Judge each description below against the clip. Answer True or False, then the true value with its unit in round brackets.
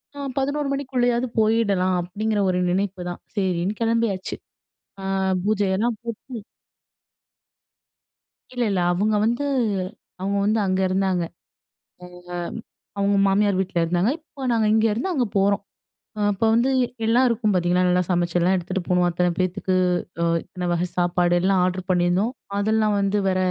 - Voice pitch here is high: True (195 Hz)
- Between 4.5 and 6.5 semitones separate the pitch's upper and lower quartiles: False (3.7 semitones)